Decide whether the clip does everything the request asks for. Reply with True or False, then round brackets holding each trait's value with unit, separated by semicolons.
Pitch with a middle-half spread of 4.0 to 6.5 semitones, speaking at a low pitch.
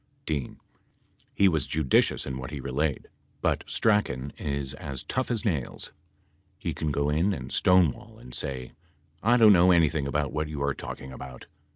True (4.5 semitones; 75 Hz)